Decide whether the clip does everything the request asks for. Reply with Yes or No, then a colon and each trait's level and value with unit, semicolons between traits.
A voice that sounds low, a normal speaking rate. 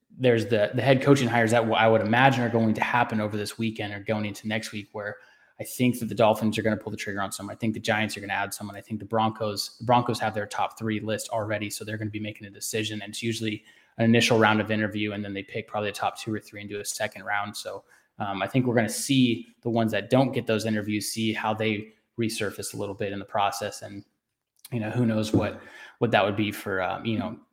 No: low, 110 Hz; fast, 275 wpm